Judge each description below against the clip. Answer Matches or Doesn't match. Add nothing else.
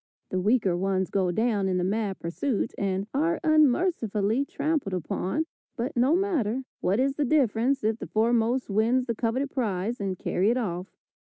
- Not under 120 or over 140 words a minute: Doesn't match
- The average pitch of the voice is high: Matches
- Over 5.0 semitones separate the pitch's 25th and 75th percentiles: Matches